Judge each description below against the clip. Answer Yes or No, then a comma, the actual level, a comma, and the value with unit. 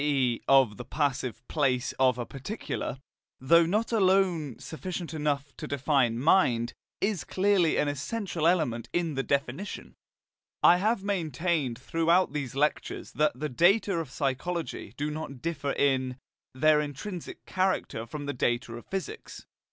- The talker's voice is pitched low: No, medium, 150 Hz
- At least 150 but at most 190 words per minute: No, average, 140 wpm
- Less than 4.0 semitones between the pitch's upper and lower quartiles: No, average, 5.1 semitones